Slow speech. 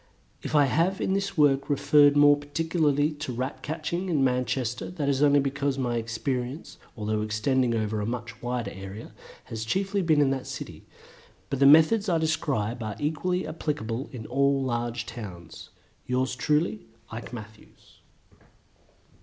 No: average, 155 wpm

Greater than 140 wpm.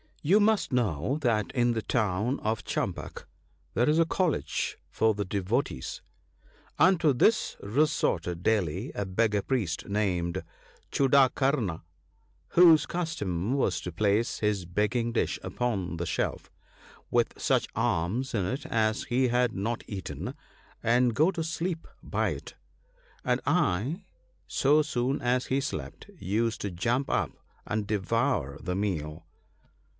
No: slow, 135 wpm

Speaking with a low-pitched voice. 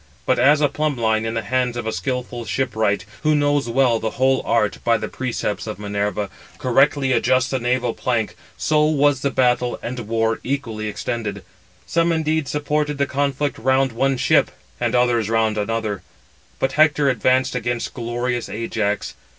Yes: low, 125 Hz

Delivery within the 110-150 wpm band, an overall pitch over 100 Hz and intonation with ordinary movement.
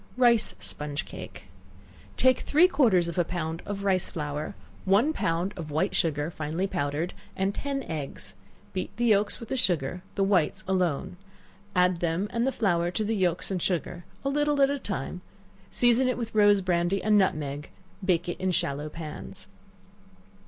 No: average, 175 wpm; medium, 185 Hz; average, 4.5 semitones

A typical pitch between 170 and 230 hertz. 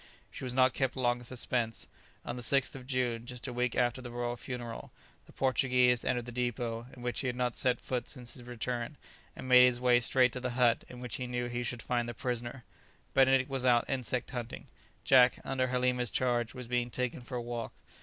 No: low, 125 Hz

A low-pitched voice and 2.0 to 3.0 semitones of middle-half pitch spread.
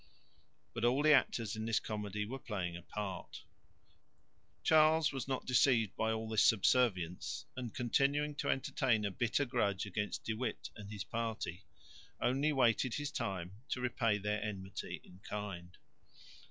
No: low, 110 Hz; average, 4.0 semitones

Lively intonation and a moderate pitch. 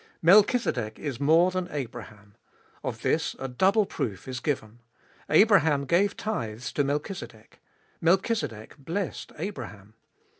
Yes: wide, 8.3 semitones; medium, 145 Hz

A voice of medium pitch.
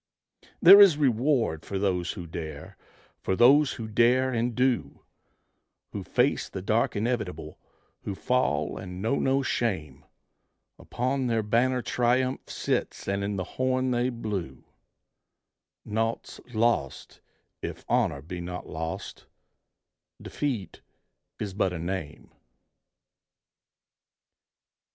No: low, 110 Hz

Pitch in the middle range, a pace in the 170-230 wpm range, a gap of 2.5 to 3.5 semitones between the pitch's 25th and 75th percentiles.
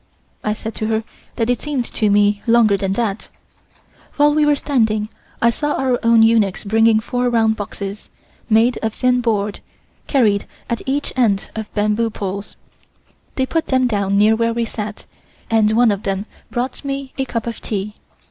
No: high, 225 Hz; average, 175 wpm; average, 2.8 semitones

